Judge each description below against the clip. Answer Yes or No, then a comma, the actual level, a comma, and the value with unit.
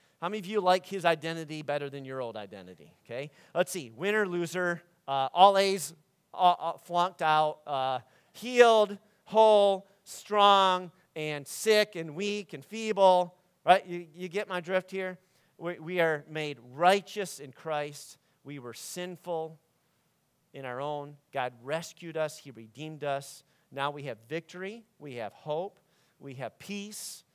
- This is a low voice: No, medium, 170 Hz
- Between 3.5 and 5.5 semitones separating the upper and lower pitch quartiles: Yes, average, 4.5 semitones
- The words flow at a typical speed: Yes, average, 150 wpm